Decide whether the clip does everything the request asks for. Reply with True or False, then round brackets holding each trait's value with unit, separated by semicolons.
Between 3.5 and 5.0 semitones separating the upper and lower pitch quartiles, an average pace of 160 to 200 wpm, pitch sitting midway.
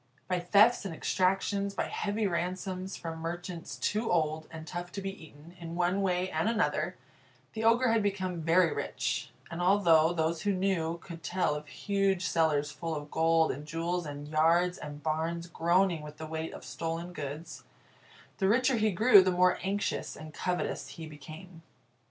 False (3.1 semitones; 175 wpm; 175 Hz)